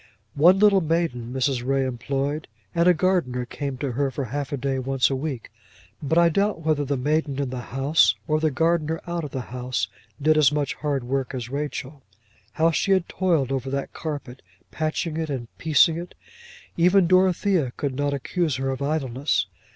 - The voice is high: No, medium, 145 Hz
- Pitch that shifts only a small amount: No, average, 3.5 semitones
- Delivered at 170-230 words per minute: Yes, average, 190 wpm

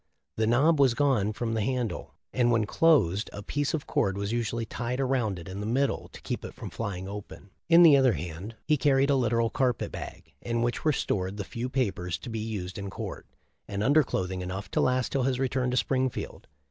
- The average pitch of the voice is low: Yes, low, 115 Hz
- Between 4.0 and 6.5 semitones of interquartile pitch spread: Yes, average, 4.7 semitones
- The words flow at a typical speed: No, fast, 220 wpm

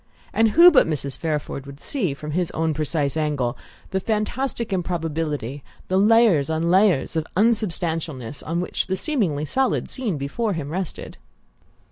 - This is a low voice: No, medium, 165 Hz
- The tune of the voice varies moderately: No, wide, 5.9 semitones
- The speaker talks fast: No, average, 150 wpm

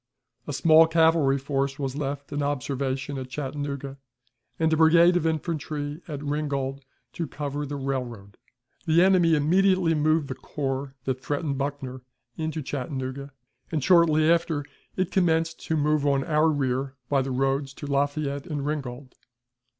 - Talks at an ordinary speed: Yes, average, 150 wpm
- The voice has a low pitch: No, medium, 145 Hz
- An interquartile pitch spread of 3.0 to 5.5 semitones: No, narrow, 2.6 semitones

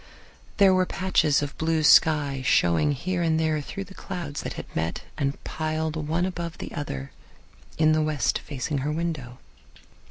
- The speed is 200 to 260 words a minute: No, average, 165 wpm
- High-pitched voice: No, medium, 155 Hz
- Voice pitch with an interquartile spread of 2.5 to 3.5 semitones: Yes, average, 2.8 semitones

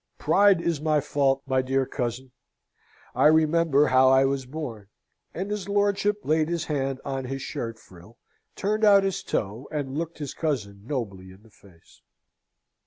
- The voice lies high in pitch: No, medium, 140 Hz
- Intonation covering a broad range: No, average, 4.6 semitones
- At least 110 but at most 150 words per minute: No, average, 165 wpm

